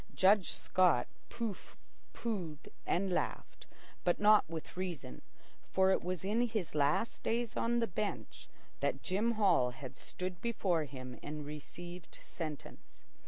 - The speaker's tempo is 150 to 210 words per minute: No, slow, 135 wpm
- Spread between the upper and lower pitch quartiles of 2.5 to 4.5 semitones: No, wide, 5.5 semitones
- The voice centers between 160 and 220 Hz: Yes, medium, 185 Hz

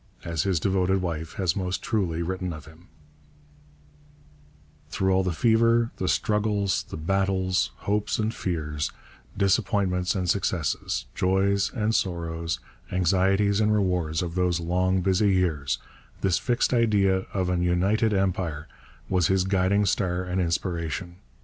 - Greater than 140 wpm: No, slow, 135 wpm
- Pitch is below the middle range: Yes, very low, 95 Hz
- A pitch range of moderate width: No, narrow, 2.3 semitones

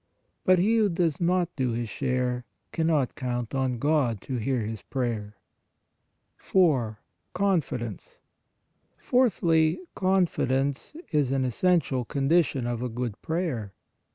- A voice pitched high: No, low, 135 Hz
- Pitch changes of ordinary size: No, wide, 5.9 semitones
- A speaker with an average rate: No, slow, 125 wpm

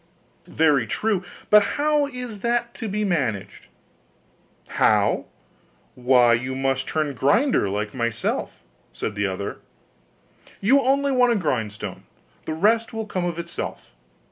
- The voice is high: No, medium, 170 Hz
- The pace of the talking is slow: Yes, slow, 130 wpm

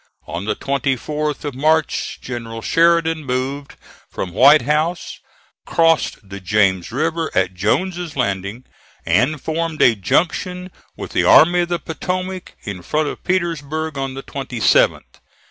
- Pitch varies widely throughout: Yes, wide, 5.7 semitones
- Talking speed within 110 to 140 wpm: Yes, slow, 135 wpm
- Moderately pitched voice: Yes, medium, 145 Hz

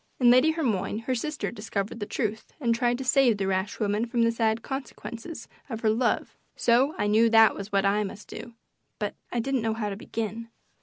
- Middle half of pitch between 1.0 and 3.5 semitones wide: Yes, narrow, 2.6 semitones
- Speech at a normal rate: No, fast, 210 wpm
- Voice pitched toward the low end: No, high, 230 Hz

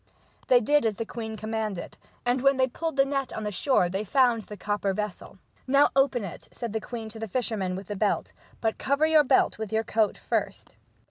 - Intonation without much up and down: No, average, 4.0 semitones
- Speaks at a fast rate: Yes, fast, 225 wpm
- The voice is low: No, high, 225 Hz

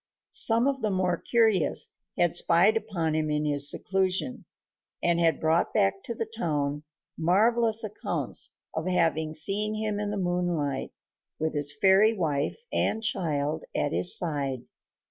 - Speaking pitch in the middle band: Yes, medium, 175 Hz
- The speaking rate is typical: Yes, average, 145 wpm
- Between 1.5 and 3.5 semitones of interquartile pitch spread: No, wide, 5.4 semitones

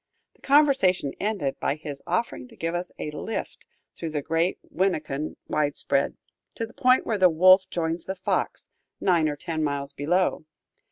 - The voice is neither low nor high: Yes, medium, 170 Hz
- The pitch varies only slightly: No, average, 3.9 semitones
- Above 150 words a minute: Yes, average, 165 wpm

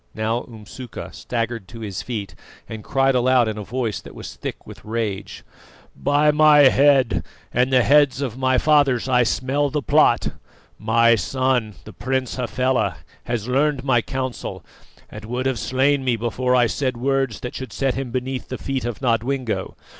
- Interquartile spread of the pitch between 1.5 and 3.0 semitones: Yes, narrow, 2.5 semitones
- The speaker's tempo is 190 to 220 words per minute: No, average, 170 wpm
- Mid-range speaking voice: No, low, 125 Hz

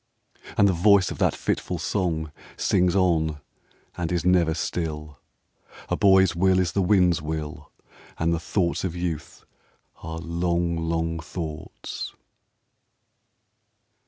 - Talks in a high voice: No, very low, 85 Hz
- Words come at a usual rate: No, slow, 125 wpm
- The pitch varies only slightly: Yes, narrow, 2.0 semitones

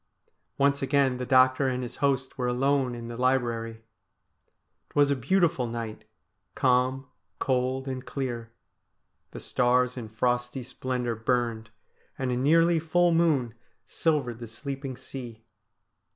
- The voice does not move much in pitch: Yes, narrow, 2.2 semitones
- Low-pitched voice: Yes, low, 130 Hz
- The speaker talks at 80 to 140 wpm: Yes, slow, 135 wpm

